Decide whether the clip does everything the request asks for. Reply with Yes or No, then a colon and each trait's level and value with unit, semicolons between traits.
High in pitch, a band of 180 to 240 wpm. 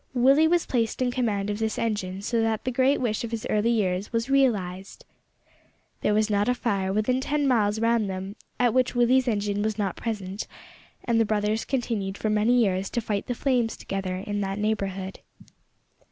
Yes: high, 220 Hz; average, 190 wpm